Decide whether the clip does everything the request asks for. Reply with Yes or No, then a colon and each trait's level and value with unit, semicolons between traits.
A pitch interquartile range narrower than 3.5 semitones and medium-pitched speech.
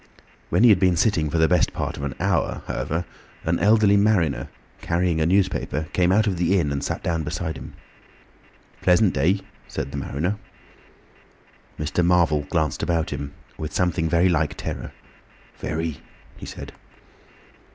No: average, 2.9 semitones; very low, 85 Hz